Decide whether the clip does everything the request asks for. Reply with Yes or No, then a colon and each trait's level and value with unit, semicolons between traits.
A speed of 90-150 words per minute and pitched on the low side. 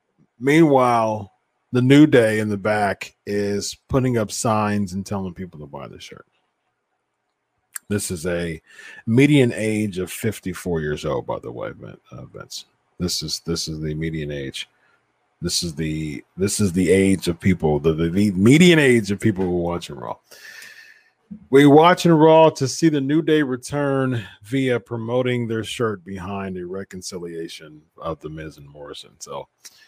No: average, 165 wpm; low, 105 Hz